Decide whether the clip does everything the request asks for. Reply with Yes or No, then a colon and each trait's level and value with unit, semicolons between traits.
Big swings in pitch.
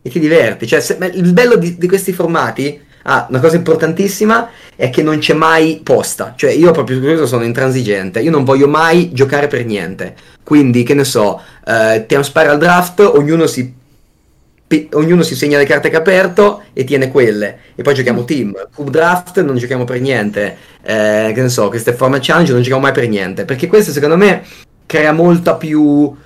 No: average, 4.6 semitones